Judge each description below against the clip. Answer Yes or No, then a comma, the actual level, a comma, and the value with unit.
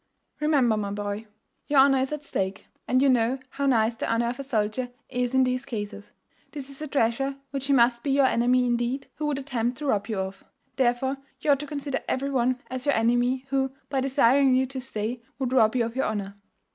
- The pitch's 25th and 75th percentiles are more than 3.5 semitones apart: No, average, 2.8 semitones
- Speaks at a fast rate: Yes, fast, 220 wpm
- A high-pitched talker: Yes, very high, 255 Hz